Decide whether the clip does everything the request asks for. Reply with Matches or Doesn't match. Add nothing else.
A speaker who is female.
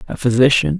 Doesn't match